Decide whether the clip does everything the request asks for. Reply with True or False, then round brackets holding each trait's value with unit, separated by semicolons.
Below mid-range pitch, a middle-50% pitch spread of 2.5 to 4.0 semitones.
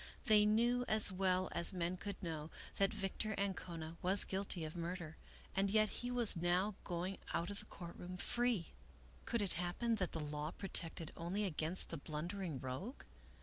False (185 Hz; 3.4 semitones)